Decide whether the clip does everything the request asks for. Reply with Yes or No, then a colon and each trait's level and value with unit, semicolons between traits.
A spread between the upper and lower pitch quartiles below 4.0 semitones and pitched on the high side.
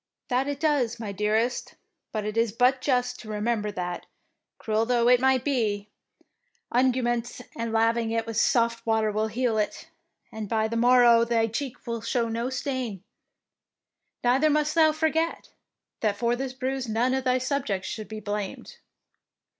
Yes: average, 2.7 semitones; high, 235 Hz